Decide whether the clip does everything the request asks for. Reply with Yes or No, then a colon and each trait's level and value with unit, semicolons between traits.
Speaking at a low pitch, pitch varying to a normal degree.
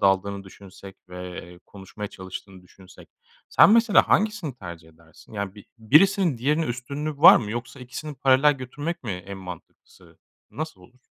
No: low, 115 Hz; wide, 7.6 semitones